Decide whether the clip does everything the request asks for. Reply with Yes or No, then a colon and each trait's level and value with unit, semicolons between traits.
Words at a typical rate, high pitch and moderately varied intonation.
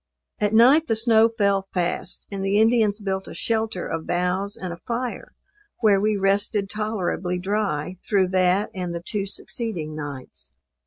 Yes: average, 160 wpm; high, 200 Hz; average, 3.2 semitones